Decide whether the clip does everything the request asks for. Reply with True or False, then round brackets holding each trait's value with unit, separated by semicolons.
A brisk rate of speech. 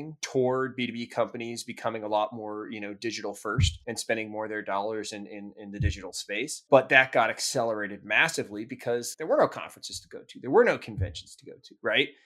True (215 wpm)